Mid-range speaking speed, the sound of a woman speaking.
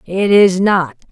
Yes: average, 160 wpm; female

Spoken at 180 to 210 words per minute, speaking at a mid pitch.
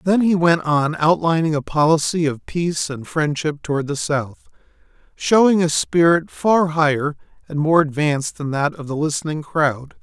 No: average, 160 wpm; medium, 155 Hz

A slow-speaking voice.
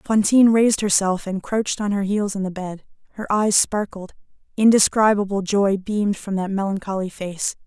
No: average, 165 wpm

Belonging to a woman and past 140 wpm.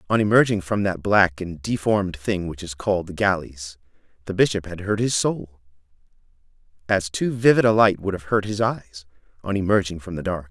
No: male; average, 195 wpm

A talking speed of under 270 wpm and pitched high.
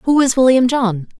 Yes: average, 200 wpm; high, 245 Hz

